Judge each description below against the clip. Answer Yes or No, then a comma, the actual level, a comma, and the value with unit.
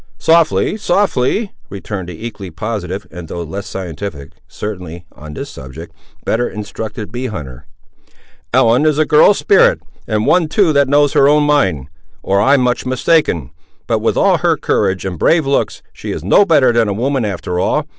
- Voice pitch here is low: Yes, low, 110 Hz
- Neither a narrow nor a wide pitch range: No, wide, 8.2 semitones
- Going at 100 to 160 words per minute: No, average, 175 wpm